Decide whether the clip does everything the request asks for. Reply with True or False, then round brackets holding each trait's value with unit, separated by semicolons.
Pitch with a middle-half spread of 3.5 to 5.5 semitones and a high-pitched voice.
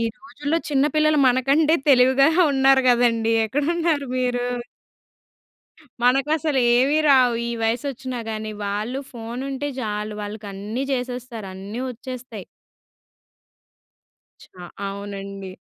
True (3.9 semitones; 250 Hz)